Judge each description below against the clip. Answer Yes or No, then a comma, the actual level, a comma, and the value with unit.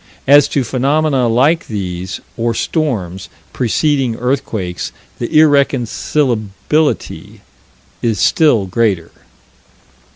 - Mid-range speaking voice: No, low, 120 Hz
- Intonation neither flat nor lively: No, wide, 5.7 semitones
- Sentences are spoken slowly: Yes, slow, 85 wpm